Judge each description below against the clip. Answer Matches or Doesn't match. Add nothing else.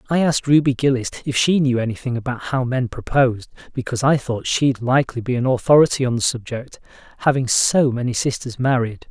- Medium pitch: Doesn't match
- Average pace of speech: Matches